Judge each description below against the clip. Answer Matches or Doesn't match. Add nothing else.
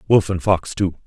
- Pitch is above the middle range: Doesn't match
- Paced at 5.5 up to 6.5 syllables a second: Doesn't match